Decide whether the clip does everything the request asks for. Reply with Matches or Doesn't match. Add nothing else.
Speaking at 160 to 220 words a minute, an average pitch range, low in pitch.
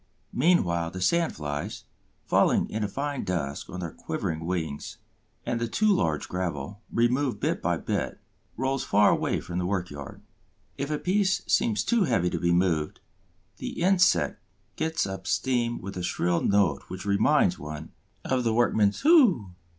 Doesn't match